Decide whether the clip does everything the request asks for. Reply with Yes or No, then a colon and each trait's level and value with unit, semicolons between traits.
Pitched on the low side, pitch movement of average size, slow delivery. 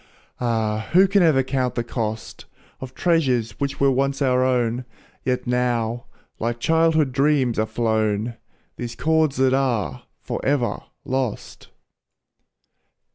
Yes: low, 125 Hz; average, 3.0 semitones; slow, 125 wpm